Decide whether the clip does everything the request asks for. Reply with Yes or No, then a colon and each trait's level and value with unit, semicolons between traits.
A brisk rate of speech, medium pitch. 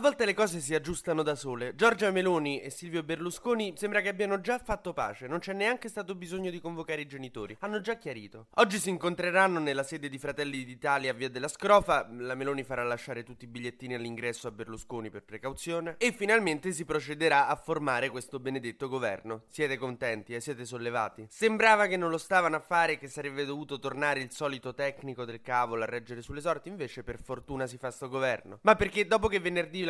Yes: fast, 205 wpm; medium, 145 Hz